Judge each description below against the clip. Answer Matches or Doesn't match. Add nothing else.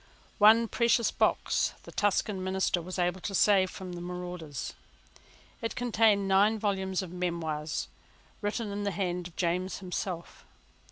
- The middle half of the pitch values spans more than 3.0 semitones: Doesn't match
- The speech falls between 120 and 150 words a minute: Matches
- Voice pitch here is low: Doesn't match